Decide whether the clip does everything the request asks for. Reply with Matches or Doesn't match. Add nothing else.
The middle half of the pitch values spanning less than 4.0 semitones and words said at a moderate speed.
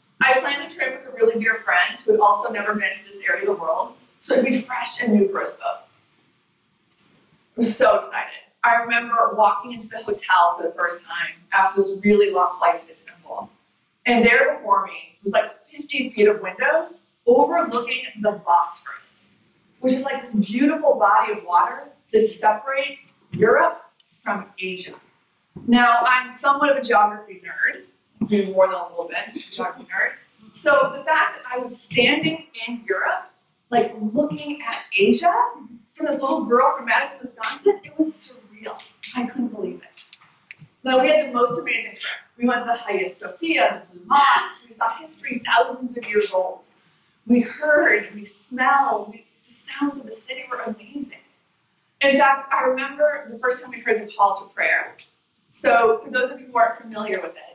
Doesn't match